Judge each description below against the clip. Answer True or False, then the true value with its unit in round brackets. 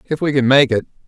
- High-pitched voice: False (135 Hz)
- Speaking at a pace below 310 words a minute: True (280 wpm)